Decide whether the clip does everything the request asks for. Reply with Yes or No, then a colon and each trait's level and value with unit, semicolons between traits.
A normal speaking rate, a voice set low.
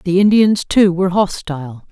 No: average, 155 wpm; medium, 185 Hz